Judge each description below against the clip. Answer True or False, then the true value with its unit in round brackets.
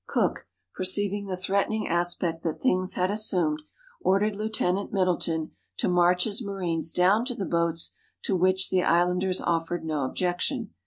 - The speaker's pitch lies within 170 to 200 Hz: True (185 Hz)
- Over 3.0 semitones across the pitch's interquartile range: False (2.5 semitones)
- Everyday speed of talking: True (150 wpm)